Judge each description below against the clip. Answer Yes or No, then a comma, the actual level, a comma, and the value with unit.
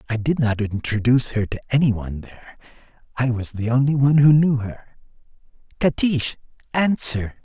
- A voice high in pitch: No, low, 125 Hz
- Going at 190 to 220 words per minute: No, average, 155 wpm